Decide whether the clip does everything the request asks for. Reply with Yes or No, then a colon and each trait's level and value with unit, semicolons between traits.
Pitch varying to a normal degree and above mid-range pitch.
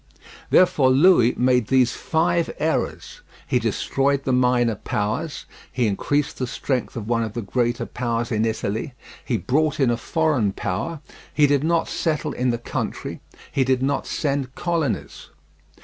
No: average, 4.0 semitones; low, 130 Hz